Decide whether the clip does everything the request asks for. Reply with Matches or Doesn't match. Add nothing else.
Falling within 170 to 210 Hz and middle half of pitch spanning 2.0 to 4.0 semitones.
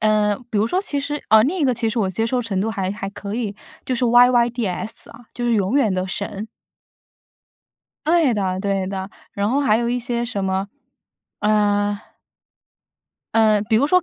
Doesn't match